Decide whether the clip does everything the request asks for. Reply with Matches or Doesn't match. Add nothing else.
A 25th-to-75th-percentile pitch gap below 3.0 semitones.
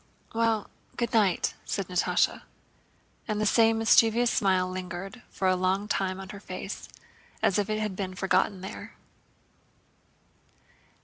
Matches